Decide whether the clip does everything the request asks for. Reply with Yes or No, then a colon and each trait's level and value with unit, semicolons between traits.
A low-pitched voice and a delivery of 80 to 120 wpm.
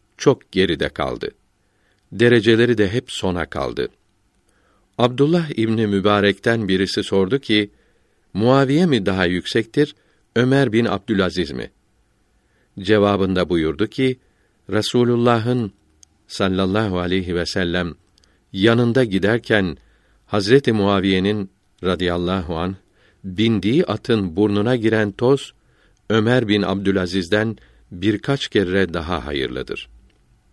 Yes: low, 105 Hz; slow, 95 wpm